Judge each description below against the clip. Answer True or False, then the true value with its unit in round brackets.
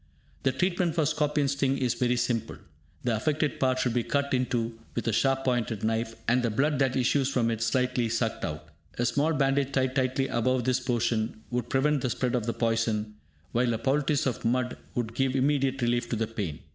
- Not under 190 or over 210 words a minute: True (205 wpm)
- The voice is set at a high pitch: False (125 Hz)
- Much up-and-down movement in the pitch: False (2.8 semitones)